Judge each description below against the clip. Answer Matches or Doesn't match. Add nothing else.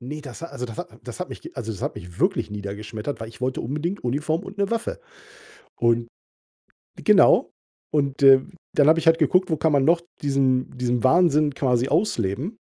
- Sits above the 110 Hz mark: Matches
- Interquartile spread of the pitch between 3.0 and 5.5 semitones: Matches